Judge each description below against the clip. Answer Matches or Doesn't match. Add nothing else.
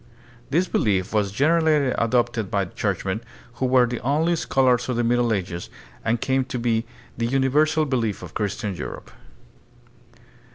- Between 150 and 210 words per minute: Matches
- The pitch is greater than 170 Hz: Doesn't match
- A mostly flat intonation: Doesn't match